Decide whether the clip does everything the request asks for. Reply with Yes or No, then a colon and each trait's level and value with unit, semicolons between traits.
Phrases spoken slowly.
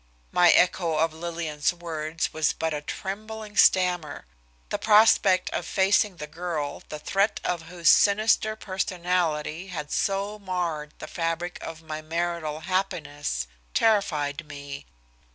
Yes: slow, 130 wpm